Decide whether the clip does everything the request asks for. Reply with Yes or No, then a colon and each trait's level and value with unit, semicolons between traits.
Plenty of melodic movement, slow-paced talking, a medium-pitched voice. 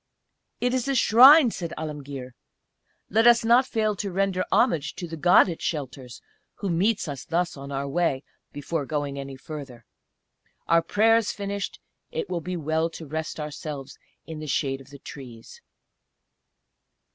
No: wide, 6.1 semitones; average, 155 wpm; medium, 160 Hz